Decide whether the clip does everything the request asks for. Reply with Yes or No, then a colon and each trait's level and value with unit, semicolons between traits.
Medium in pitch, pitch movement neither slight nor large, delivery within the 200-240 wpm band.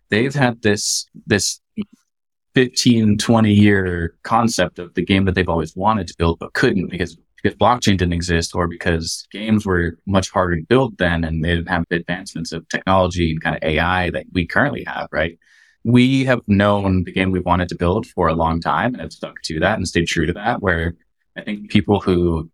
No: very low, 90 Hz; average, 3.6 semitones; fast, 205 wpm